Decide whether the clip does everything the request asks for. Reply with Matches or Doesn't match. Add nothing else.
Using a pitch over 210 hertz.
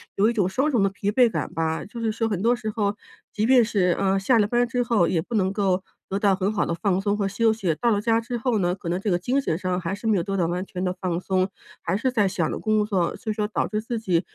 Doesn't match